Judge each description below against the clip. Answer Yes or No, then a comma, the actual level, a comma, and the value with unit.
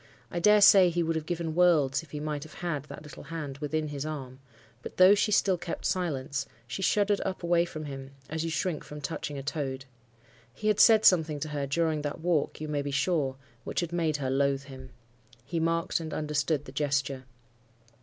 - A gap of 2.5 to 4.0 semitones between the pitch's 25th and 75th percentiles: Yes, average, 3.4 semitones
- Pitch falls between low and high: Yes, medium, 155 Hz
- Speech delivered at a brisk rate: Yes, fast, 210 wpm